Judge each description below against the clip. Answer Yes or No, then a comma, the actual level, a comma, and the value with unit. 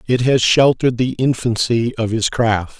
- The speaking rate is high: No, average, 170 wpm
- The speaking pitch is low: Yes, low, 120 Hz